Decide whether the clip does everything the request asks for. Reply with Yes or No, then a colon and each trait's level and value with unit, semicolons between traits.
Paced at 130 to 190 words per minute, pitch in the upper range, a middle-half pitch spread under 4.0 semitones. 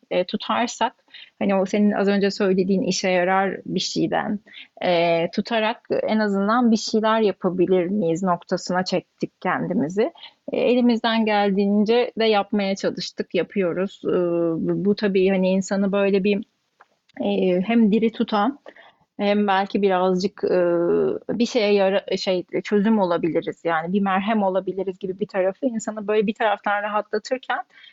Yes: average, 135 wpm; high, 200 Hz; average, 2.9 semitones